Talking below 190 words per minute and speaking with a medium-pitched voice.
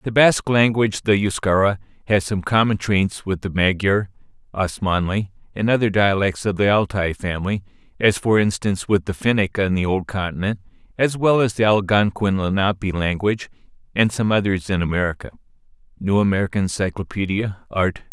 No: average, 145 wpm; low, 100 Hz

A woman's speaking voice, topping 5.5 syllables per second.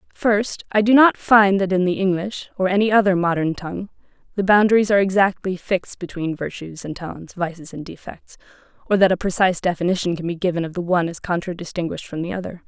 Yes: female; 6.3 syllables/s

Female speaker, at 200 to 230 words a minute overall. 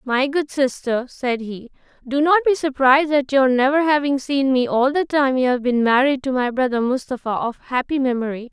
Yes: female; fast, 205 wpm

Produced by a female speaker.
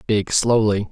No: male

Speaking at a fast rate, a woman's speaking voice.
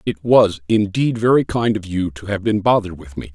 No: fast, 235 wpm; male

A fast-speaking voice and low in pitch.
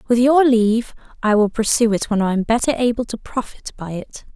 No: fast, 220 wpm; high, 225 Hz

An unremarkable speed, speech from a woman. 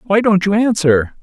No: average, 195 wpm; male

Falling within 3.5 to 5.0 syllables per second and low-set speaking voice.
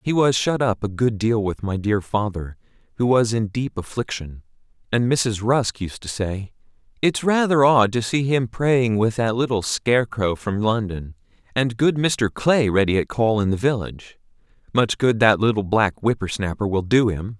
Yes: 4.7 syllables/s; low, 115 Hz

